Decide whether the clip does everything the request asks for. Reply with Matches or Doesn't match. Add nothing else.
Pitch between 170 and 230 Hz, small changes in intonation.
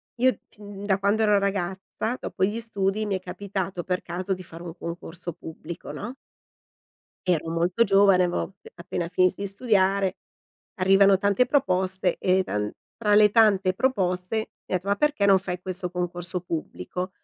Matches